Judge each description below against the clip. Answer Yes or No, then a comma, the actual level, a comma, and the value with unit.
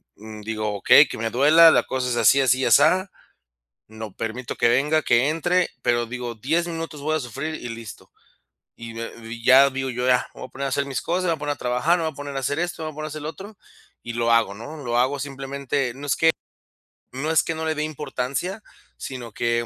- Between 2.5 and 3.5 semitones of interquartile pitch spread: No, average, 4.7 semitones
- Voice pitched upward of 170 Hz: No, low, 135 Hz